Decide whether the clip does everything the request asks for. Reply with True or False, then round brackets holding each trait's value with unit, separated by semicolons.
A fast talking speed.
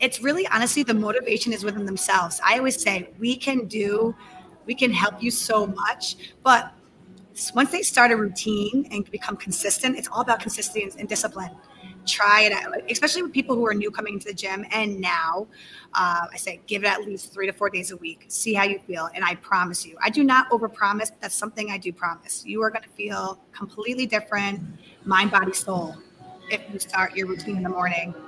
True (210 wpm)